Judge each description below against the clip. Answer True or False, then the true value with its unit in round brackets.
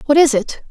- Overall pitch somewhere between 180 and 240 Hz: False (270 Hz)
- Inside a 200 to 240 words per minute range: False (255 wpm)